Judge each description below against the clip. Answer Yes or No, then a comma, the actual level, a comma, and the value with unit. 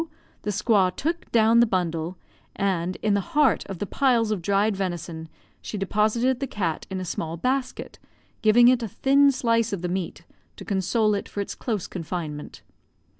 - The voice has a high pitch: Yes, high, 205 Hz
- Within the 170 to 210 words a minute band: Yes, average, 175 wpm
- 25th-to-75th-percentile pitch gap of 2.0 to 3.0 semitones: No, average, 4.4 semitones